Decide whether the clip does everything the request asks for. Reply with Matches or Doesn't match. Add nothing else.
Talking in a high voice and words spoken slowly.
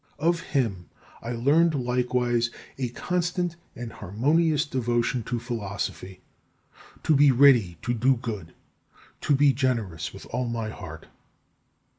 Doesn't match